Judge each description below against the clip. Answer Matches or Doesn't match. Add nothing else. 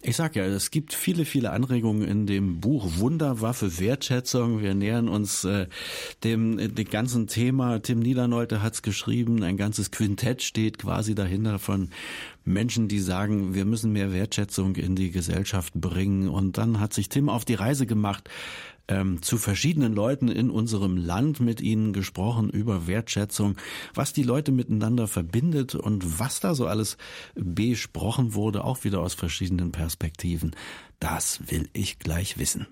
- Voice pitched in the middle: Doesn't match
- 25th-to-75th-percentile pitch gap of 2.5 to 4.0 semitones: Matches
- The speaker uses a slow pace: Doesn't match